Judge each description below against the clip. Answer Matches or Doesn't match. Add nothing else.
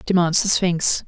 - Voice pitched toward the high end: Doesn't match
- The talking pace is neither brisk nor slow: Matches